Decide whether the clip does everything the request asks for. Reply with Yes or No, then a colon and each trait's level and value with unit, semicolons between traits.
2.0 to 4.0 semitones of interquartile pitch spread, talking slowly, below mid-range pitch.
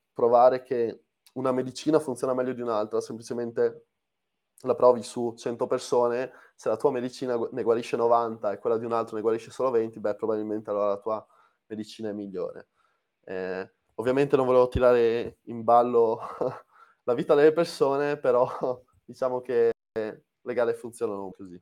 No: average, 2.8 semitones; average, 155 wpm; low, 115 Hz